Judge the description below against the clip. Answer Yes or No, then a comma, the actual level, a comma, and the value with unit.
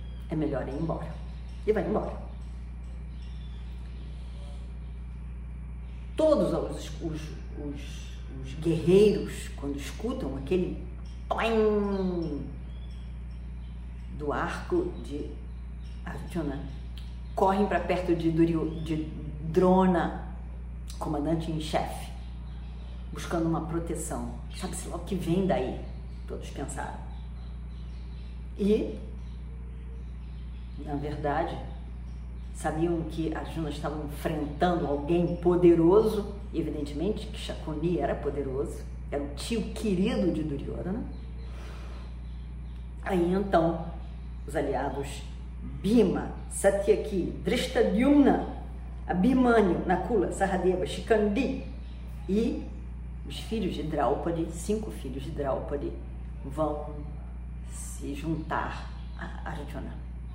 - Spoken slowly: Yes, slow, 85 wpm